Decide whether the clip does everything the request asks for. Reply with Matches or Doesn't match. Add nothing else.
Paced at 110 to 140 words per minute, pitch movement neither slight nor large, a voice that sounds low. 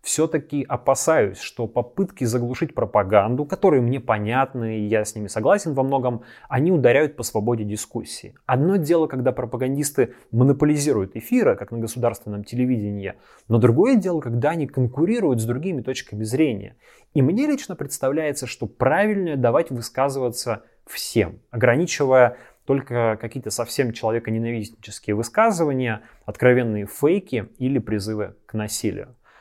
Matches